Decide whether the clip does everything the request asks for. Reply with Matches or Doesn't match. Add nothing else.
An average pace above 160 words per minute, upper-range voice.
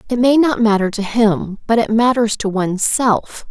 Matches